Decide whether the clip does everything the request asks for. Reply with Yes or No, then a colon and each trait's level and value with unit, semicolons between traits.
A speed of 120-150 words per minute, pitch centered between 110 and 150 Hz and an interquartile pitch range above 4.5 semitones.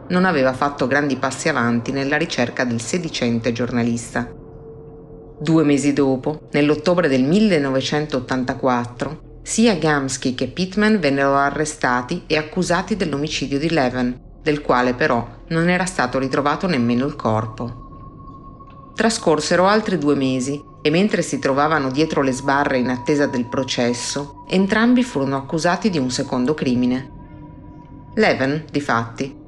No: average, 130 wpm; medium, 140 Hz; average, 3.2 semitones